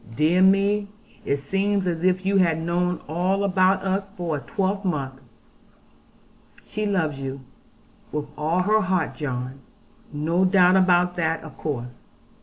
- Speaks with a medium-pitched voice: Yes, medium, 180 Hz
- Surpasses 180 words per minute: No, average, 140 wpm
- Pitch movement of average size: Yes, average, 4.0 semitones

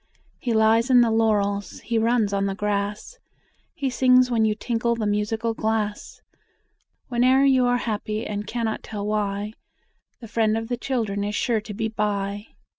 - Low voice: No, high, 220 Hz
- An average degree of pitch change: No, narrow, 2.2 semitones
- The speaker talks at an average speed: Yes, average, 170 wpm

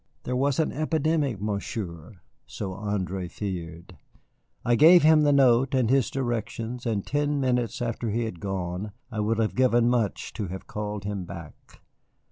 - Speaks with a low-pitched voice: Yes, low, 115 Hz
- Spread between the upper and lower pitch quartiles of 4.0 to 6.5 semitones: Yes, average, 4.7 semitones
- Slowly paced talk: No, average, 160 wpm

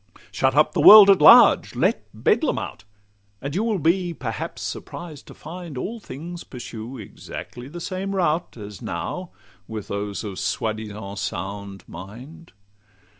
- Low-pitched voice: Yes, low, 130 Hz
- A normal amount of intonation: No, wide, 8.8 semitones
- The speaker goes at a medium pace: Yes, average, 150 wpm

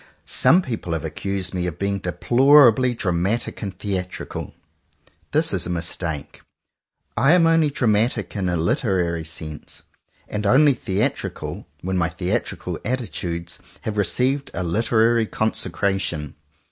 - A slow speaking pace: Yes, slow, 130 wpm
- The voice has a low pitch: Yes, low, 100 Hz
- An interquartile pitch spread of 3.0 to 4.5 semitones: No, average, 5.2 semitones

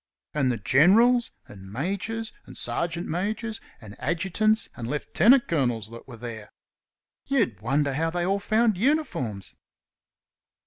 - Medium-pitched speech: Yes, medium, 165 Hz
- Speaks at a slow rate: Yes, slow, 130 wpm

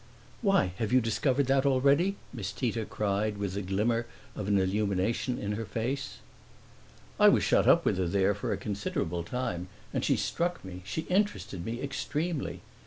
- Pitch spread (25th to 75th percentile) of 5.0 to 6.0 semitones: Yes, average, 5.3 semitones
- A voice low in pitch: Yes, low, 110 Hz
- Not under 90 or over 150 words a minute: No, average, 175 wpm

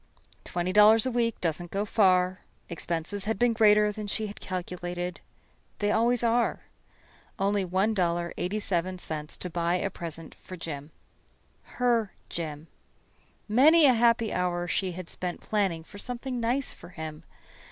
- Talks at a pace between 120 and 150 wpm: Yes, average, 140 wpm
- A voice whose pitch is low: No, high, 190 Hz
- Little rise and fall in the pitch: No, average, 4.1 semitones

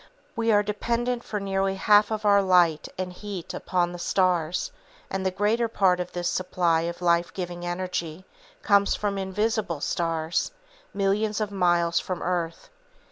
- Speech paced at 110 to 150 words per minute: No, average, 160 wpm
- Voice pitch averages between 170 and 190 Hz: Yes, medium, 185 Hz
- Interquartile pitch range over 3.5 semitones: No, average, 2.9 semitones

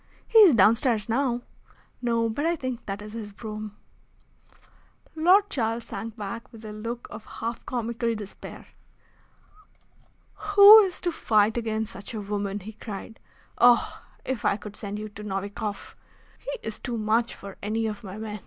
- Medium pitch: No, high, 225 Hz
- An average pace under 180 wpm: Yes, average, 160 wpm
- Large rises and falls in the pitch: No, narrow, 2.5 semitones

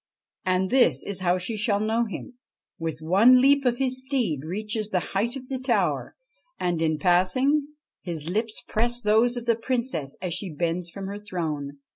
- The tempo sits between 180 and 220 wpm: Yes, average, 185 wpm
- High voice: Yes, high, 205 Hz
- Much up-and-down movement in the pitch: Yes, wide, 5.7 semitones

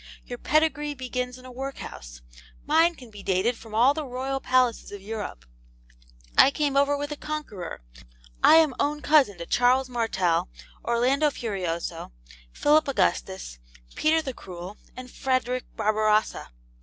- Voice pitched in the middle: No, very high, 250 Hz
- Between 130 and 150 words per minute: Yes, average, 145 wpm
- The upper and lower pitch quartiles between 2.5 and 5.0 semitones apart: No, wide, 5.5 semitones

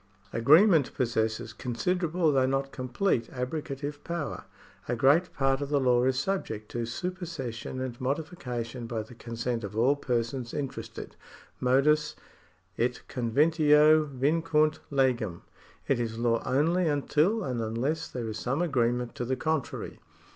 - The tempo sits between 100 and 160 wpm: Yes, slow, 135 wpm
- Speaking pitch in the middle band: No, low, 130 Hz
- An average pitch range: Yes, average, 4.3 semitones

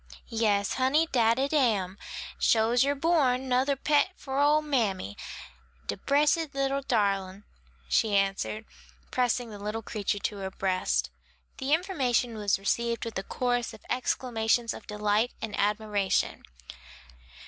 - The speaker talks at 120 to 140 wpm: Yes, slow, 135 wpm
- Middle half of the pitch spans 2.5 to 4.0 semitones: No, average, 4.7 semitones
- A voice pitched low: No, high, 230 Hz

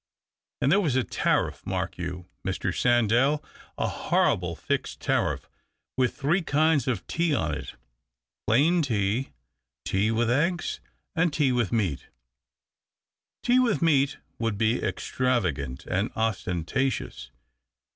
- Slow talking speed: Yes, slow, 130 wpm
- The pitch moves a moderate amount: No, wide, 7.1 semitones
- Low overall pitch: Yes, low, 120 Hz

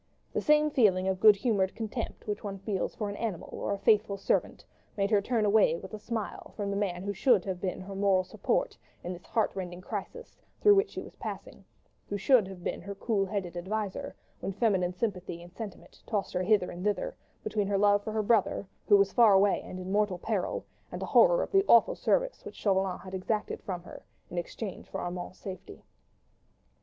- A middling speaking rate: No, fast, 210 wpm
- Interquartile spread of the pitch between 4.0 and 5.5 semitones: No, average, 2.7 semitones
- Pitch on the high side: Yes, high, 200 Hz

